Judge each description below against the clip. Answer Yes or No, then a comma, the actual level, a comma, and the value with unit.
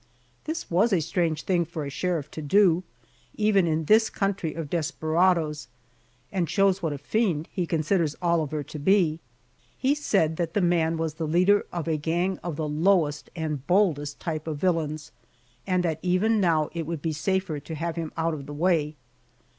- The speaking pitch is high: No, medium, 165 Hz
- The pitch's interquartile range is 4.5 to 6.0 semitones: No, average, 3.0 semitones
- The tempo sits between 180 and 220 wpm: Yes, average, 185 wpm